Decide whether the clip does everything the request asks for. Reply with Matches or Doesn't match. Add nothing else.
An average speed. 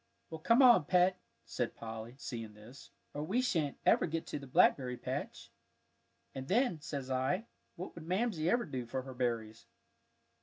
Matches